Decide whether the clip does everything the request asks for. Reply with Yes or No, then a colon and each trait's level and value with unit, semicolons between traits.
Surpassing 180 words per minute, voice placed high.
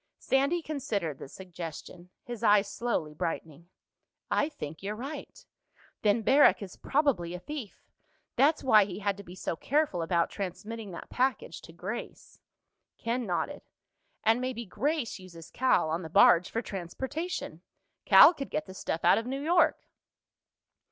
No: average, 150 wpm; high, 210 Hz